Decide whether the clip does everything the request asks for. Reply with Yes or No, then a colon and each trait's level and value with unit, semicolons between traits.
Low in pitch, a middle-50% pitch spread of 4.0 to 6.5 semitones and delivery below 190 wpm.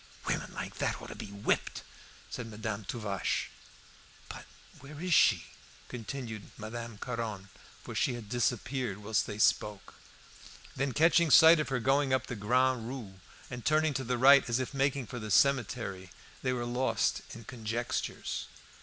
No: low, 120 Hz; average, 3.6 semitones; average, 160 wpm